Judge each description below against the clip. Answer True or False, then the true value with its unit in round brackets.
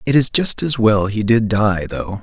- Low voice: True (110 Hz)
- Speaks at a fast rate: True (245 wpm)